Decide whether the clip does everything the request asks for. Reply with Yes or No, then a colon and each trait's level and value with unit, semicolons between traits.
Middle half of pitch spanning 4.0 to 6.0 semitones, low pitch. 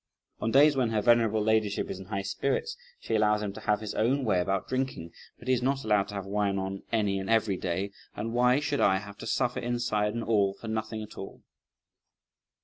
No: average, 3.3 semitones; low, 110 Hz